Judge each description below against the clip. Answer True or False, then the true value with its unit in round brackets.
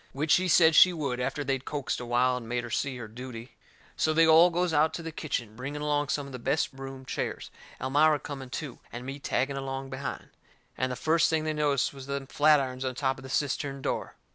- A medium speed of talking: False (230 wpm)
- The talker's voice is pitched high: False (140 Hz)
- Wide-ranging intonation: False (2.8 semitones)